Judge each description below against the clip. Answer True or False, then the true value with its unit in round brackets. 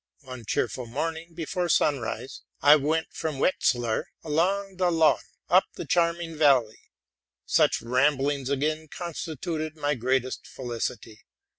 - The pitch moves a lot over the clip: False (4.2 semitones)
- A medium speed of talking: False (120 wpm)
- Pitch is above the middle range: False (150 Hz)